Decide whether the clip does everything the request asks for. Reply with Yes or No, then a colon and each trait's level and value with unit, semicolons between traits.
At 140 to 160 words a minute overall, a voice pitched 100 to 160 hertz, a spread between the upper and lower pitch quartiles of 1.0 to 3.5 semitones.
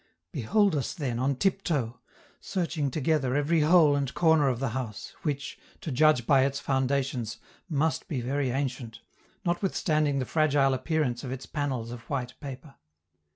Yes: average, 155 wpm; medium, 140 Hz; average, 3.2 semitones